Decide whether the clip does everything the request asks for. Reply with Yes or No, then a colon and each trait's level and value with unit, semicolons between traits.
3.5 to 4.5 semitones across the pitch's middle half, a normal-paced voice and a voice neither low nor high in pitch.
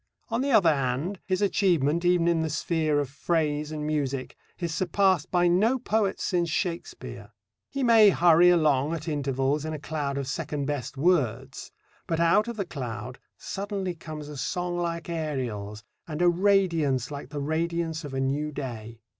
Yes: average, 3.8 semitones; average, 170 wpm; medium, 160 Hz